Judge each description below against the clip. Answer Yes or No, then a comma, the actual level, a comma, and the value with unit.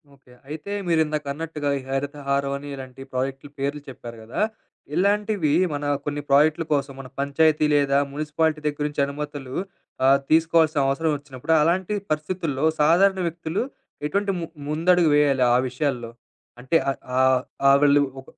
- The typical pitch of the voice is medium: Yes, medium, 145 Hz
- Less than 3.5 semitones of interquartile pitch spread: Yes, narrow, 2.6 semitones